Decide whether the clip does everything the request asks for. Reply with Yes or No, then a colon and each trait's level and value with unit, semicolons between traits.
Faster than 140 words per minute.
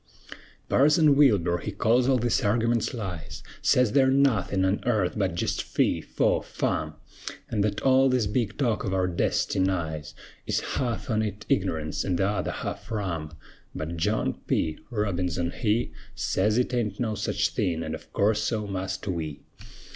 Yes: average, 160 wpm